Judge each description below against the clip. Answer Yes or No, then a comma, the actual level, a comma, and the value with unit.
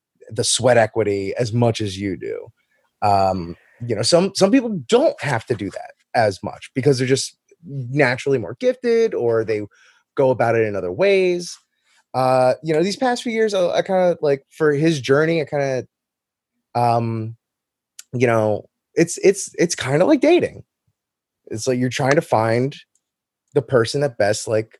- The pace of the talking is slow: No, average, 180 wpm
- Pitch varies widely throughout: Yes, wide, 7.6 semitones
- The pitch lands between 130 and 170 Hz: Yes, low, 135 Hz